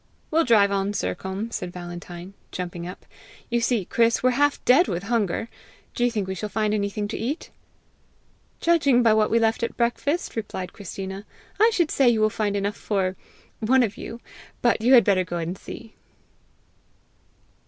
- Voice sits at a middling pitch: No, high, 215 Hz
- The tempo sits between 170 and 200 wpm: Yes, average, 175 wpm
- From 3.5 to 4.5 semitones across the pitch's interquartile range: Yes, average, 3.8 semitones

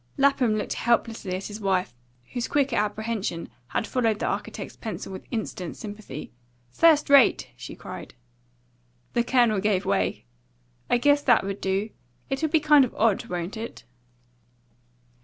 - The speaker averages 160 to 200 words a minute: No, average, 145 wpm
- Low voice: No, high, 220 Hz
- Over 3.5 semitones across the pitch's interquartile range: Yes, average, 4.5 semitones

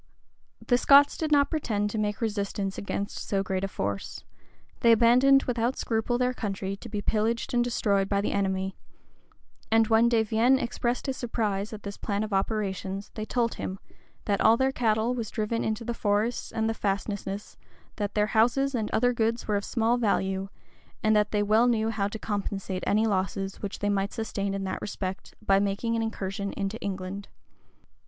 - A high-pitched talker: Yes, high, 215 Hz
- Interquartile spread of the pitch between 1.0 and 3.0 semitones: Yes, average, 2.7 semitones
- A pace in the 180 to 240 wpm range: Yes, average, 185 wpm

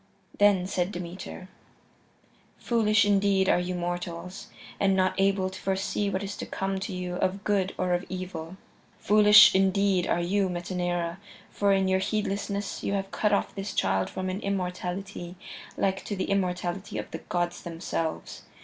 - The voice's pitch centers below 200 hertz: Yes, high, 190 Hz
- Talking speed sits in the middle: Yes, average, 160 wpm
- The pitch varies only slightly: Yes, narrow, 1.8 semitones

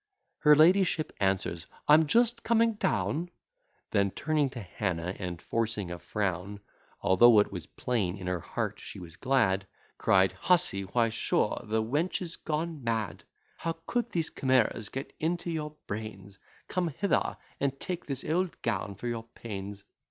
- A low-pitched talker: Yes, low, 115 Hz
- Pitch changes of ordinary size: No, wide, 8.3 semitones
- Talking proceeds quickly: No, average, 155 wpm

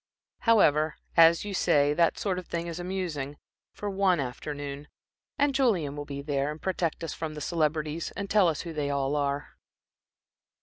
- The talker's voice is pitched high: No, medium, 160 Hz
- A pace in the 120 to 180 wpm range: Yes, average, 175 wpm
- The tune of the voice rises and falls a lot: No, average, 3.9 semitones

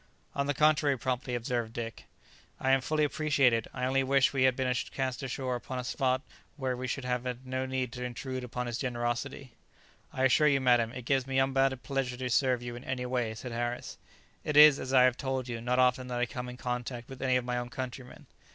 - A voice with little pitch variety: Yes, narrow, 1.4 semitones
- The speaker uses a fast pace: Yes, fast, 225 wpm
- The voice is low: Yes, low, 125 Hz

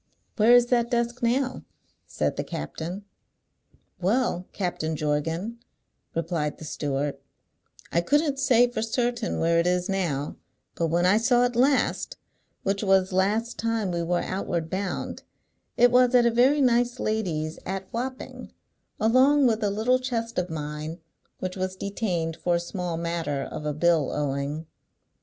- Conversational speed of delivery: Yes, average, 150 wpm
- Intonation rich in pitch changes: Yes, wide, 6.2 semitones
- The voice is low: No, high, 195 Hz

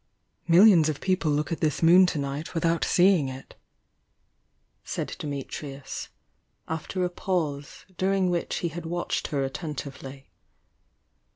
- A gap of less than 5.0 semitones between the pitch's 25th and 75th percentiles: Yes, average, 3.8 semitones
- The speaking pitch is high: No, medium, 160 Hz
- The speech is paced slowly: Yes, slow, 125 wpm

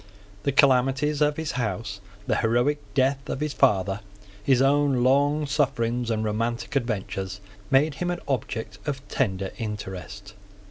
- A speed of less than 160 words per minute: Yes, average, 140 wpm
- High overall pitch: No, low, 125 Hz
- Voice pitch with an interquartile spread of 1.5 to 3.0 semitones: No, average, 4.7 semitones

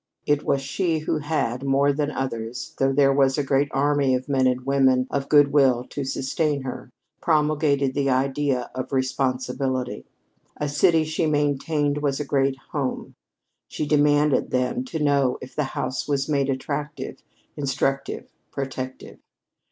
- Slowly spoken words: No, average, 150 wpm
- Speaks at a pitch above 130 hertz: Yes, medium, 140 Hz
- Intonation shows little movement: Yes, narrow, 1.9 semitones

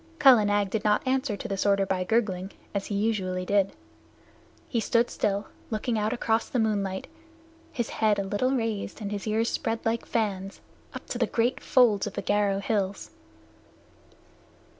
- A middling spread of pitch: No, narrow, 2.3 semitones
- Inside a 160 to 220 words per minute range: Yes, average, 170 wpm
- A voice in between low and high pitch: No, high, 210 Hz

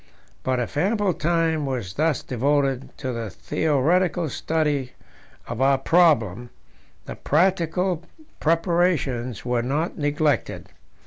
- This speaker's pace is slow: Yes, slow, 110 wpm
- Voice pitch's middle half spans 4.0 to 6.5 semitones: Yes, average, 4.7 semitones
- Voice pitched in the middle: Yes, medium, 150 Hz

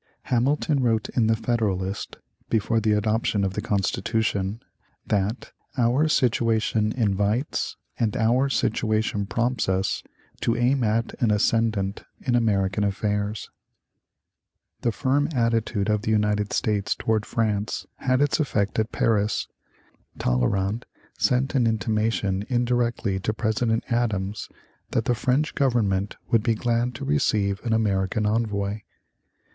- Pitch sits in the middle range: No, low, 110 Hz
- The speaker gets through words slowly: Yes, slow, 125 wpm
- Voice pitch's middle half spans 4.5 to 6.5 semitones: No, average, 2.7 semitones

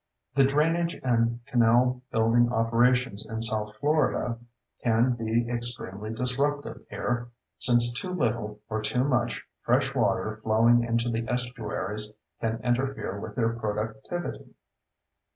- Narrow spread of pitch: Yes, narrow, 2.0 semitones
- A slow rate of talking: Yes, slow, 120 wpm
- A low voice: Yes, low, 120 Hz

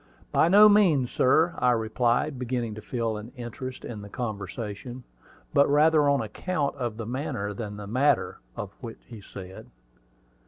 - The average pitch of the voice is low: Yes, low, 120 Hz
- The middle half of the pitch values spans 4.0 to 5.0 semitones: Yes, average, 4.6 semitones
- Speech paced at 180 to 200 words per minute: No, average, 160 wpm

